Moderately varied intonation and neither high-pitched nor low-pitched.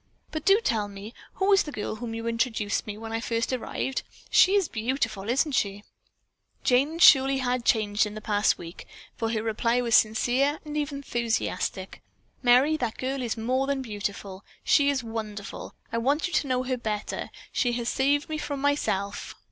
No: average, 4.2 semitones; high, 240 Hz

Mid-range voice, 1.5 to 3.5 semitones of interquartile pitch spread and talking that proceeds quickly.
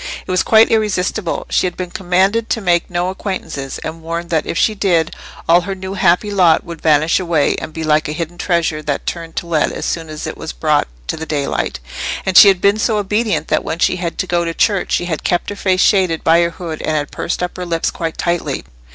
Yes: medium, 175 Hz; average, 2.8 semitones; fast, 240 wpm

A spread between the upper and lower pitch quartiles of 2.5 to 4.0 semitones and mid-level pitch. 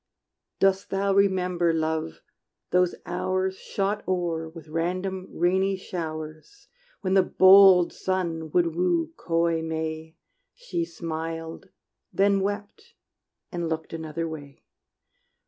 Yes: average, 2.8 semitones; medium, 175 Hz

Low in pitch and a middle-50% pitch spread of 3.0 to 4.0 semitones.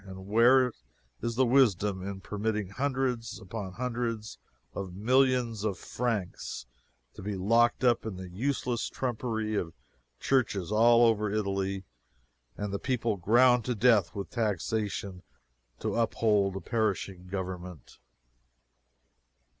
Yes: low, 110 Hz; average, 3.5 semitones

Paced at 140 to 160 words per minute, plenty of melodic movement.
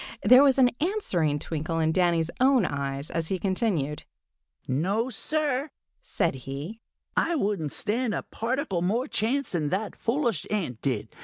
Yes: average, 150 wpm; wide, 8.2 semitones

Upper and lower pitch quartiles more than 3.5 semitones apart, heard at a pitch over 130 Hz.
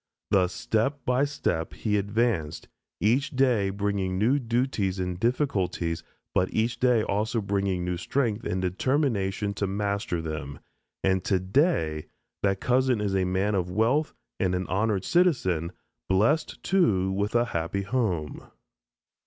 No: average, 4.6 semitones; low, 100 Hz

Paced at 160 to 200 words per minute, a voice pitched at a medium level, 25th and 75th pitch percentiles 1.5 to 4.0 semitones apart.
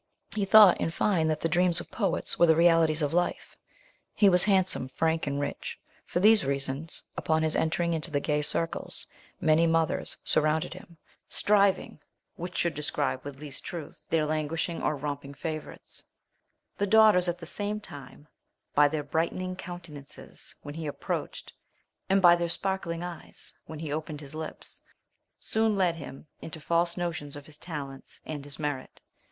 Yes: average, 165 wpm; medium, 160 Hz; average, 3.0 semitones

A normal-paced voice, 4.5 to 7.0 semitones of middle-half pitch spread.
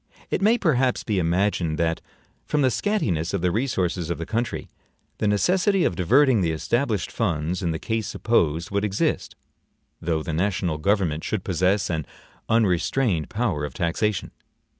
Yes: average, 160 wpm; wide, 5.6 semitones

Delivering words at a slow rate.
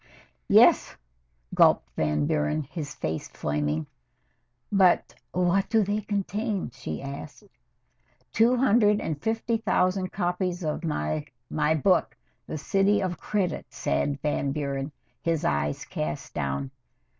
Yes: slow, 120 wpm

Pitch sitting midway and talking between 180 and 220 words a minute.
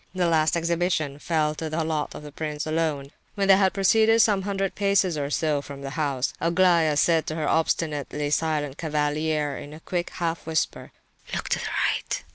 Yes: medium, 160 Hz; average, 190 wpm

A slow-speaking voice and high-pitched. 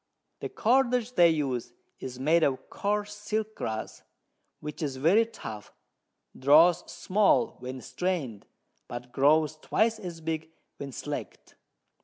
No: slow, 125 wpm; medium, 160 Hz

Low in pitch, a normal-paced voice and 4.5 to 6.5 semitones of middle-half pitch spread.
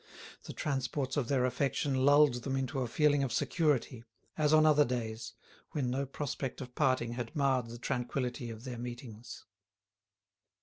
No: low, 130 Hz; average, 160 wpm; average, 2.7 semitones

